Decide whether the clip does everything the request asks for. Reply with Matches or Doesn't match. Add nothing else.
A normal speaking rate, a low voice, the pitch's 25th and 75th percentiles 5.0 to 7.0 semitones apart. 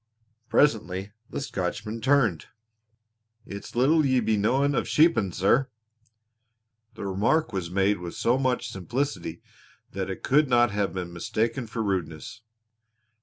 Doesn't match